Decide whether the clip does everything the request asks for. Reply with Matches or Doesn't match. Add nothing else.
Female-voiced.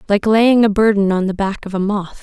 Matches